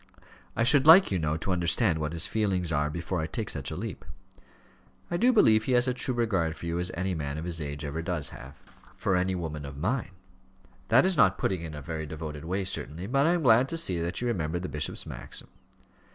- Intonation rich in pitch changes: Yes, wide, 6.4 semitones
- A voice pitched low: Yes, very low, 90 Hz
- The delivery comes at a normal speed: No, fast, 245 wpm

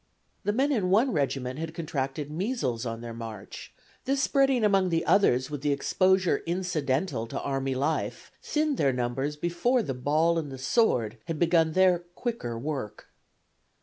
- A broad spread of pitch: Yes, wide, 6.3 semitones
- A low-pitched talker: No, medium, 155 Hz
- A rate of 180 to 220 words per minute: No, average, 155 wpm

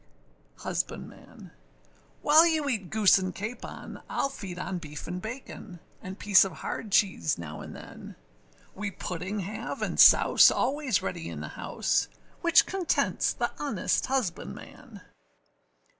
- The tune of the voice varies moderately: No, wide, 6.0 semitones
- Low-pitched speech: No, high, 200 Hz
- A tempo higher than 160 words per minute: No, slow, 135 wpm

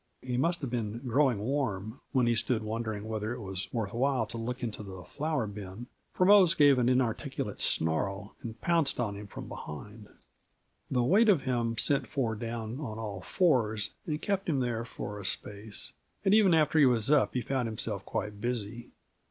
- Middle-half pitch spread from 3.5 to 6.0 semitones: Yes, average, 4.4 semitones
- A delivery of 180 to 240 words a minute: Yes, average, 190 wpm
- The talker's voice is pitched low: Yes, low, 120 Hz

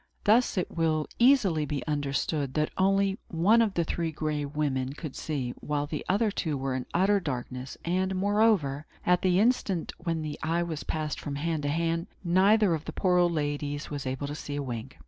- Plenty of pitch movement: No, average, 4.5 semitones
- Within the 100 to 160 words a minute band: No, average, 200 wpm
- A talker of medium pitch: Yes, medium, 160 Hz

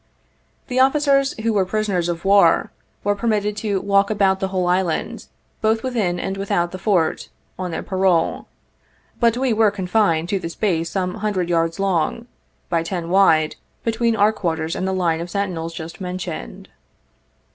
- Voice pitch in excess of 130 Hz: Yes, high, 190 Hz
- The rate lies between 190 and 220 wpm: No, average, 165 wpm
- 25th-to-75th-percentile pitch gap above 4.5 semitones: No, average, 3.6 semitones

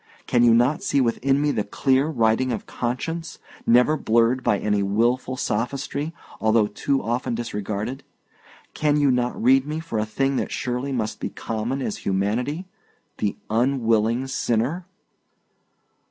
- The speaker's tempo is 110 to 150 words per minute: Yes, average, 145 wpm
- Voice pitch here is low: Yes, low, 125 Hz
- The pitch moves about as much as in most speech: Yes, average, 3.5 semitones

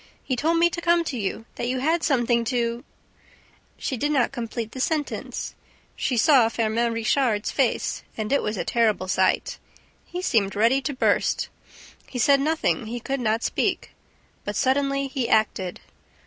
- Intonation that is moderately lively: Yes, average, 3.7 semitones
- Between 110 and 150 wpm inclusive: No, average, 170 wpm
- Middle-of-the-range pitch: No, high, 245 Hz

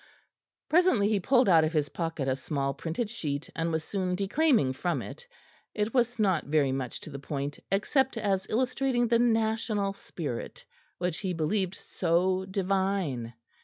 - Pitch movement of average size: No, wide, 6.0 semitones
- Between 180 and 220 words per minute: No, average, 160 wpm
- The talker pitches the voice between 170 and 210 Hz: Yes, high, 190 Hz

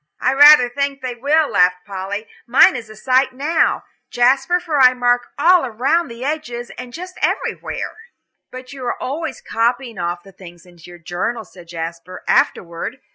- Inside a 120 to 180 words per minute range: Yes, average, 170 wpm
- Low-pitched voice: No, high, 245 Hz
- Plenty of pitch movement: Yes, wide, 6.2 semitones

